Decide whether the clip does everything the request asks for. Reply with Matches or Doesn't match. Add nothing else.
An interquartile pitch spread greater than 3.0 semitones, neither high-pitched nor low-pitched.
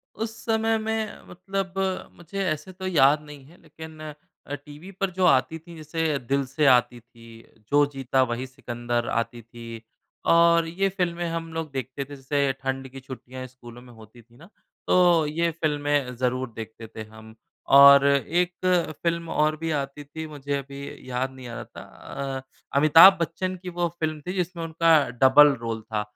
Matches